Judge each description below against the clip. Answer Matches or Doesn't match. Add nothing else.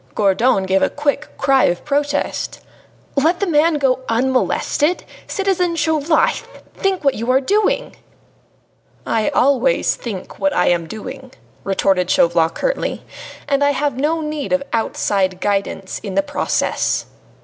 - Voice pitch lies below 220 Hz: Doesn't match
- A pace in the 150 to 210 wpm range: Doesn't match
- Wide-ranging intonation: Matches